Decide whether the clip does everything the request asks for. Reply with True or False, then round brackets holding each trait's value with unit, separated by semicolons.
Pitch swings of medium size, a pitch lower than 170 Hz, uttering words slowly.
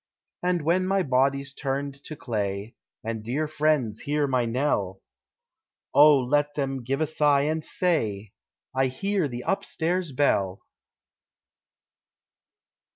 True (3.9 semitones; 140 Hz; 120 wpm)